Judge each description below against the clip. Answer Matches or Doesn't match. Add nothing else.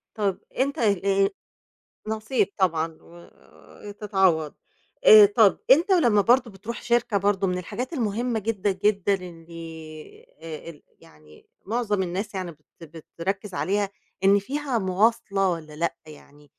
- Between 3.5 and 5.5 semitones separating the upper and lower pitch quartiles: Matches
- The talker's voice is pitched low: Doesn't match